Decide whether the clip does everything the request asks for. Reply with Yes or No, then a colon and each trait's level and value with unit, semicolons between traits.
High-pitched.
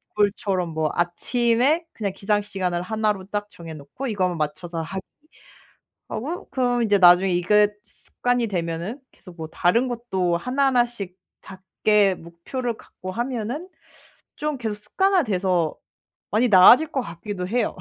Yes: high, 205 Hz